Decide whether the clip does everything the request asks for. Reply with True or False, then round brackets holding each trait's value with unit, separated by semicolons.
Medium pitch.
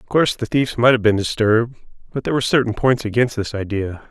False (115 Hz)